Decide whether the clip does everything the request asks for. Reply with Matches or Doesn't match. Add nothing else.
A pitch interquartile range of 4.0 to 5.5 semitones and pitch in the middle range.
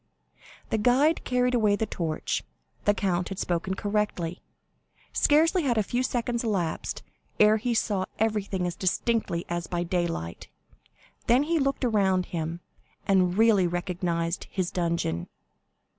Doesn't match